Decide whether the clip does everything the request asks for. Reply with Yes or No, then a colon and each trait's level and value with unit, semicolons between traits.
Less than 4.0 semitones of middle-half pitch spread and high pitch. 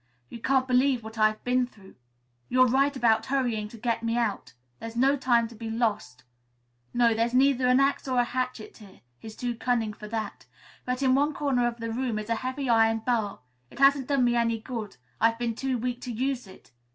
Yes: narrow, 2.4 semitones; high, 240 Hz